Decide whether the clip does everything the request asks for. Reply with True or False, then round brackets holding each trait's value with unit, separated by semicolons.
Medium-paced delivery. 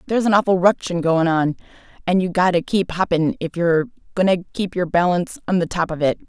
False (230 wpm)